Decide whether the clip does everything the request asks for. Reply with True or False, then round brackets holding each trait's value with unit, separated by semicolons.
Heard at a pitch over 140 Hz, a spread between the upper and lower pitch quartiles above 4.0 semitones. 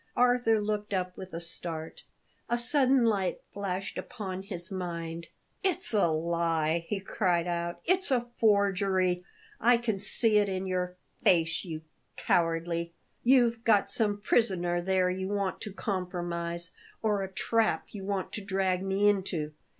False (190 Hz; 3.3 semitones)